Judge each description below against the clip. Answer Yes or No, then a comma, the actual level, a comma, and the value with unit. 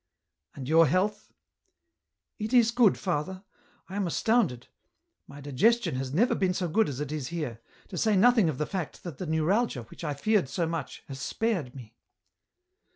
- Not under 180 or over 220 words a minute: Yes, average, 190 wpm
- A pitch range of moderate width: No, wide, 6.7 semitones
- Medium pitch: Yes, medium, 170 Hz